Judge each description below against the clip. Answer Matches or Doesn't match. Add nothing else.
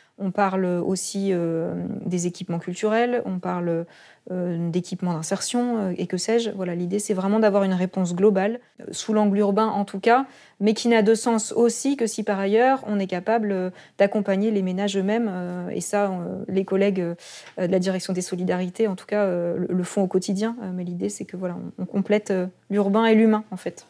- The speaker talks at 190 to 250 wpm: Matches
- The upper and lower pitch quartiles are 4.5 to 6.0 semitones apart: Doesn't match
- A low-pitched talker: Doesn't match